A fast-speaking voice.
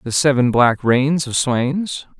No: average, 165 wpm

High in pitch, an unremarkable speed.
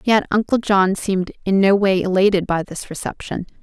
Yes: high, 195 Hz; average, 180 wpm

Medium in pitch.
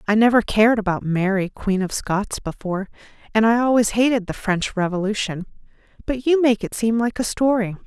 No: high, 215 Hz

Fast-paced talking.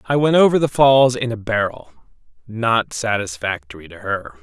No: average, 150 wpm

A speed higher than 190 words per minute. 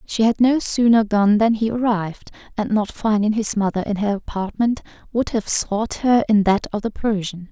Yes: average, 200 wpm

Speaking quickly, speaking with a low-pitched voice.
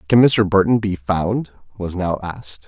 No: average, 180 wpm; very low, 95 Hz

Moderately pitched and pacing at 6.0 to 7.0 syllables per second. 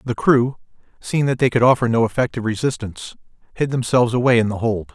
No: low, 120 Hz; 6.5 syllables/s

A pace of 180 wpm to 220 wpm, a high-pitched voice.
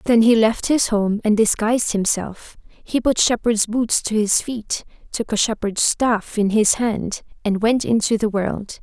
Yes: average, 185 wpm; high, 220 Hz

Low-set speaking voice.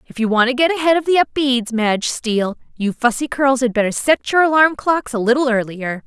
No: very high, 255 Hz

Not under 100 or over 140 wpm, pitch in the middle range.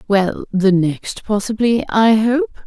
No: slow, 135 wpm; high, 215 Hz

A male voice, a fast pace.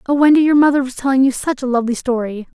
No: female; fast, 255 wpm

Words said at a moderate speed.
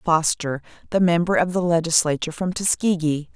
Yes: average, 145 wpm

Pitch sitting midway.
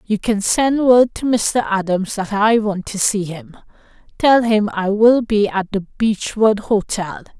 No: high, 210 Hz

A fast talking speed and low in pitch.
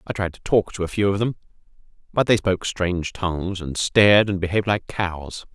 Yes: fast, 215 wpm; very low, 95 Hz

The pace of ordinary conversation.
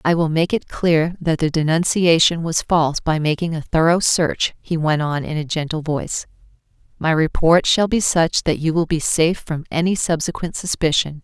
Yes: average, 190 wpm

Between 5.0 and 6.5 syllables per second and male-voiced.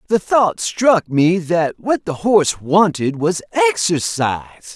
No: 4.0 syllables/s; male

